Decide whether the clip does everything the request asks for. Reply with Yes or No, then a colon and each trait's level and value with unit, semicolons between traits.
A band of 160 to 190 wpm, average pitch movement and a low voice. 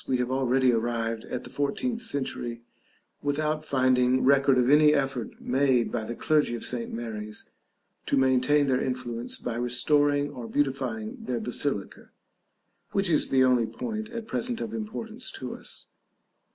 No: average, 150 wpm; average, 3.4 semitones; low, 130 Hz